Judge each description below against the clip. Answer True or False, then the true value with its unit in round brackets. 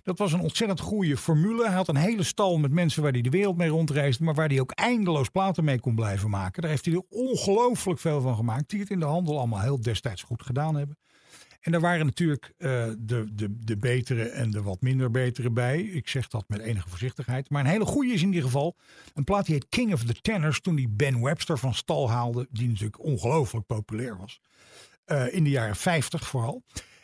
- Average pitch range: False (6.1 semitones)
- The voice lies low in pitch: False (145 Hz)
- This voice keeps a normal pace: False (230 wpm)